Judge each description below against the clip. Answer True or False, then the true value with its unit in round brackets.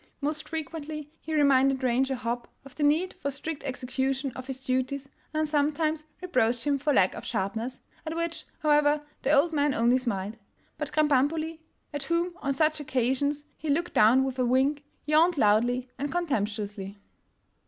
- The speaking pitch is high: True (280 Hz)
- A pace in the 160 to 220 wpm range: True (165 wpm)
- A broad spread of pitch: False (3.2 semitones)